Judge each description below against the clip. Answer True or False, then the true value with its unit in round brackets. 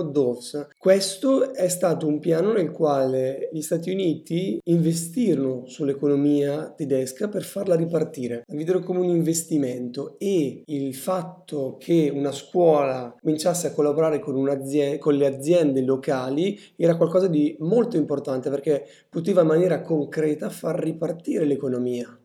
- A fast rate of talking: False (130 wpm)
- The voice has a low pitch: False (155 Hz)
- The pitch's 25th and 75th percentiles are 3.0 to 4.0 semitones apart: True (3.5 semitones)